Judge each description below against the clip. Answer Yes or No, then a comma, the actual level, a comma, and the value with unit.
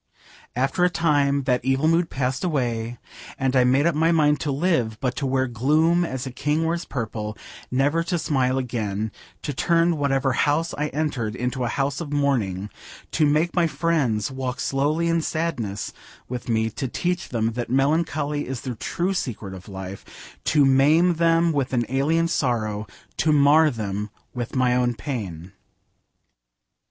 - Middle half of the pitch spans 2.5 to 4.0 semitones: No, average, 4.5 semitones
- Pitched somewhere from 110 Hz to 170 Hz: Yes, low, 135 Hz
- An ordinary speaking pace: Yes, average, 165 wpm